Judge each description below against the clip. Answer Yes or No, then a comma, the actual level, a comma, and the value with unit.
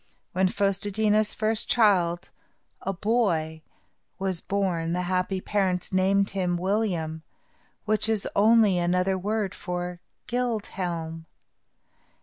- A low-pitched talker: No, high, 190 Hz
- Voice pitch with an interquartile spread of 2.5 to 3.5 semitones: Yes, average, 2.9 semitones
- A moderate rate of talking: No, slow, 125 wpm